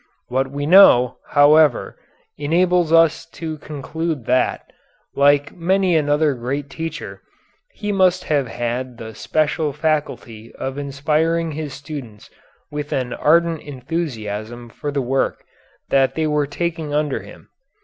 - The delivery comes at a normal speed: No, slow, 130 wpm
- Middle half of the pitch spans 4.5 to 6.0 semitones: No, average, 3.4 semitones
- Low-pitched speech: No, medium, 145 Hz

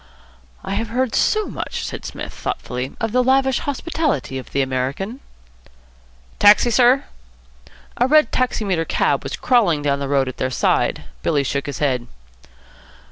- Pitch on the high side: Yes, high, 200 Hz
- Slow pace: No, average, 150 wpm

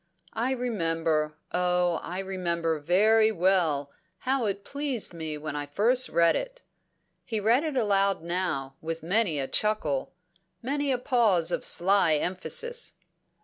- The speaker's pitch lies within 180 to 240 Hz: Yes, medium, 185 Hz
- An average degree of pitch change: No, wide, 5.9 semitones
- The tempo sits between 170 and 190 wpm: No, average, 140 wpm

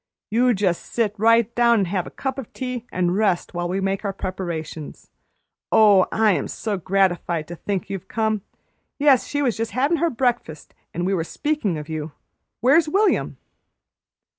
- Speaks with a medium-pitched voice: No, high, 205 Hz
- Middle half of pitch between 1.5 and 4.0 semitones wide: No, average, 5.1 semitones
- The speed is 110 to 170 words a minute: No, average, 180 wpm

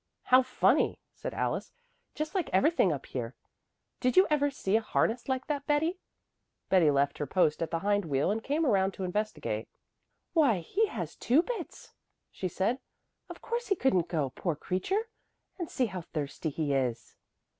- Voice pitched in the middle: No, high, 205 Hz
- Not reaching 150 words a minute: No, average, 175 wpm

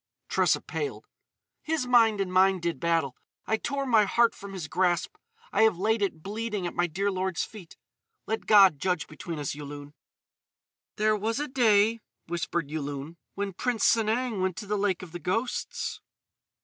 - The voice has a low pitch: No, high, 195 Hz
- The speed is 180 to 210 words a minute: No, average, 170 wpm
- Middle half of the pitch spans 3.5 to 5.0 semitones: Yes, average, 4.4 semitones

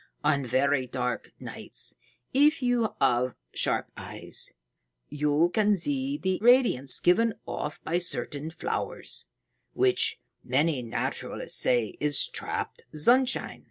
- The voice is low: No, medium, 165 Hz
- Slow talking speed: Yes, slow, 115 wpm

